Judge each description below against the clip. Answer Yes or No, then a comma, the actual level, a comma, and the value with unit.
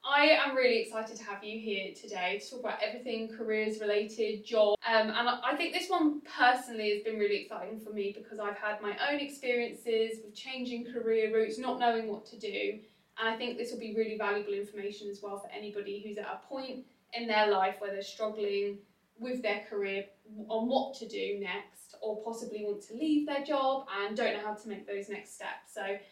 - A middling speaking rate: No, fast, 210 wpm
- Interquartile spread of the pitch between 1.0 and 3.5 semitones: Yes, average, 2.9 semitones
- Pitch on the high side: Yes, high, 220 Hz